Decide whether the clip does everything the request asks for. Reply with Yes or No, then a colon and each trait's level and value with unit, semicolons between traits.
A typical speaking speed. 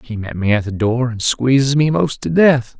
No: fast, 260 wpm